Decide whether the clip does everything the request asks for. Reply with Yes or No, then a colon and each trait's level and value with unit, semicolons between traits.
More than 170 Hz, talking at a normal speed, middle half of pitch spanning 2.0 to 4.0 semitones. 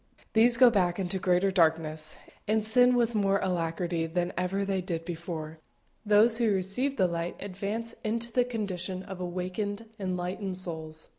Yes: high, 190 Hz; average, 155 wpm; average, 3.6 semitones